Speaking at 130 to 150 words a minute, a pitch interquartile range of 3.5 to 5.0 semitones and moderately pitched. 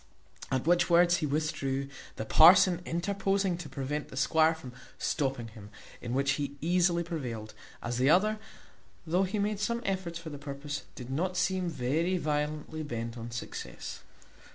No: average, 160 wpm; average, 4.6 semitones; medium, 155 Hz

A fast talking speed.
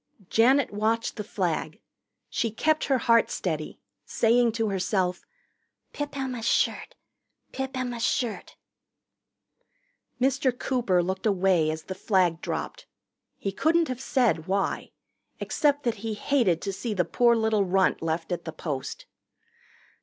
No: average, 140 wpm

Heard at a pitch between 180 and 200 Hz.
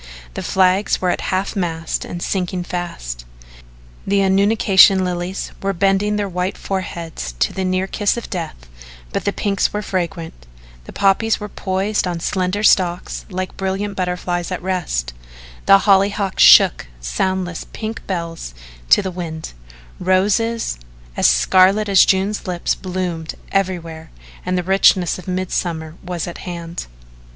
Yes: medium, 185 Hz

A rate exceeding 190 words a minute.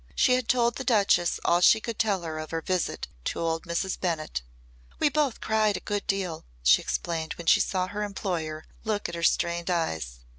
Yes: average, 200 wpm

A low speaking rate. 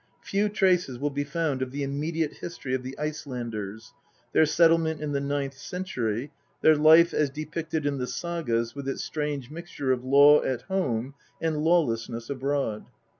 No: average, 165 wpm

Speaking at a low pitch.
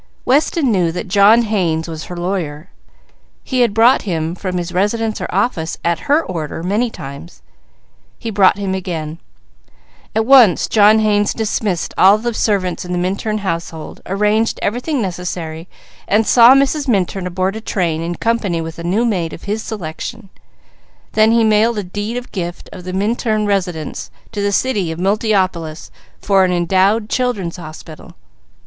No: high, 195 Hz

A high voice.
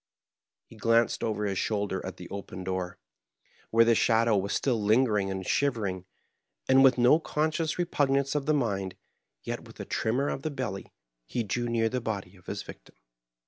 No: low, 115 Hz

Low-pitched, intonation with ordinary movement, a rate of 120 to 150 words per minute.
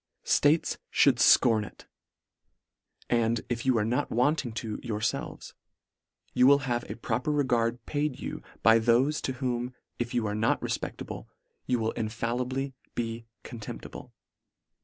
No: low, 120 Hz; narrow, 2.3 semitones; average, 140 wpm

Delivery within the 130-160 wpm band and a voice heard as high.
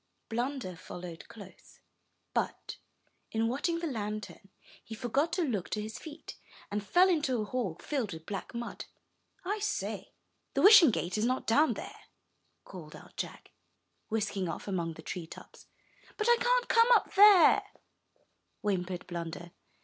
Yes: average, 150 wpm; high, 225 Hz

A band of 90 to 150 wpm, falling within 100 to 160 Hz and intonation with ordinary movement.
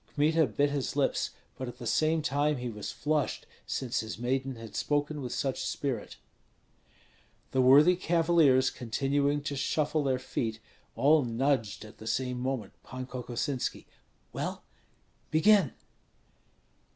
Yes: slow, 135 wpm; low, 135 Hz; average, 3.0 semitones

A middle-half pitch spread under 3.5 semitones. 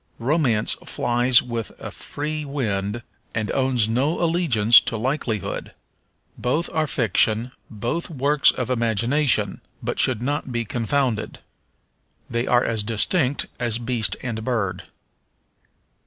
No: average, 3.8 semitones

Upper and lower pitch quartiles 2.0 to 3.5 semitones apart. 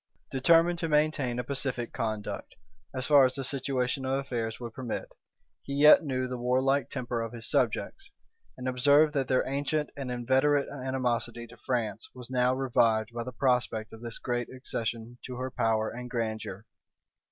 Yes: narrow, 2.5 semitones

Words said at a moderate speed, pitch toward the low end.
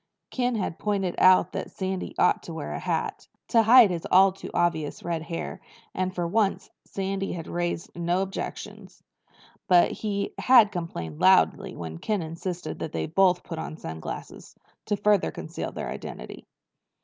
No: average, 160 wpm; medium, 185 Hz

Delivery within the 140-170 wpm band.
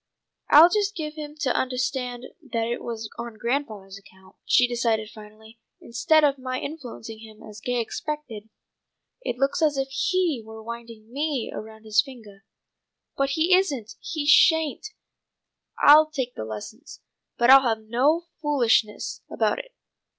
Yes: average, 150 wpm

